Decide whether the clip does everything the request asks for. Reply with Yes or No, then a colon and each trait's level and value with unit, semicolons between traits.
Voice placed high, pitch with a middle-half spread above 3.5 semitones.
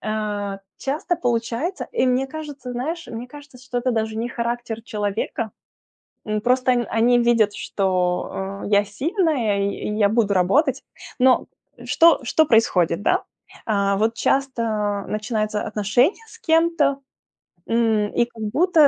Yes: high, 235 Hz; average, 4.2 semitones